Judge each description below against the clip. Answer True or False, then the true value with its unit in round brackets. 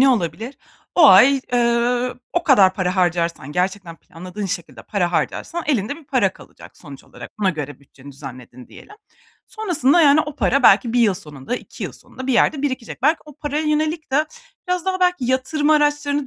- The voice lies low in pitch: False (250 Hz)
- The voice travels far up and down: True (8.4 semitones)